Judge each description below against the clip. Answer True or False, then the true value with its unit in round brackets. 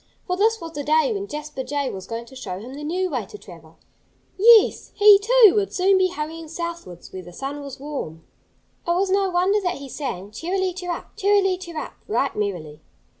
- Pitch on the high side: True (320 Hz)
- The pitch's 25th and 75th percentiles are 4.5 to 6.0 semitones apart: False (6.7 semitones)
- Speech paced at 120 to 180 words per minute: False (200 wpm)